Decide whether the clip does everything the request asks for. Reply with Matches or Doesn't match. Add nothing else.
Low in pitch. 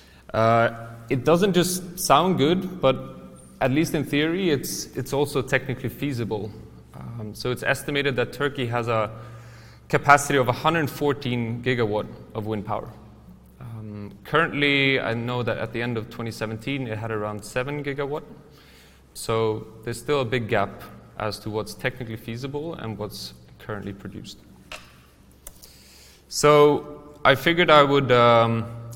Matches